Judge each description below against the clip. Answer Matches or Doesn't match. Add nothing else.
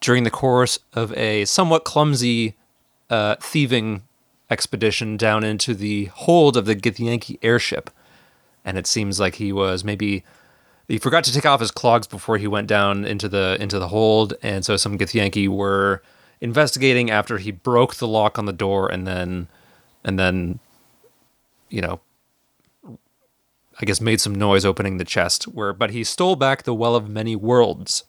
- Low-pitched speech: Matches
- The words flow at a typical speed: Matches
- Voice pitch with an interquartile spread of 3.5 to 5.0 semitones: Doesn't match